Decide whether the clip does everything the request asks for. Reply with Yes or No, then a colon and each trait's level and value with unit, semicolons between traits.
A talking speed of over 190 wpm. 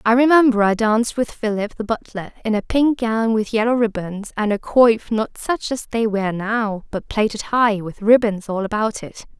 Yes: fast, 205 wpm